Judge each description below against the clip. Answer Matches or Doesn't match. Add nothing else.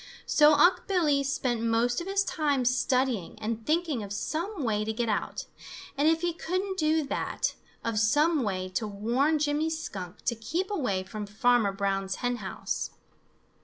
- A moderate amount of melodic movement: Doesn't match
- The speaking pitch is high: Matches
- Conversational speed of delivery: Matches